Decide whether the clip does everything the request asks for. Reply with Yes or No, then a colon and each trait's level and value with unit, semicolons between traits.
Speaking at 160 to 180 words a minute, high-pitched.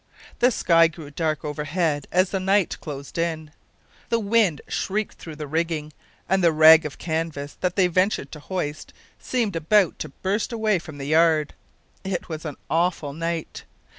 No: average, 165 wpm; medium, 165 Hz